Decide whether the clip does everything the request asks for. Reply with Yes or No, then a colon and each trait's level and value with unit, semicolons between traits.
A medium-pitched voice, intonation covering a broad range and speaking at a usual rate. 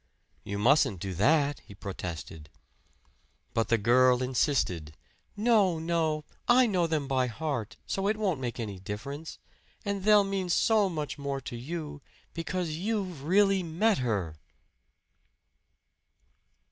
No: medium, 150 Hz; wide, 7.9 semitones; slow, 130 wpm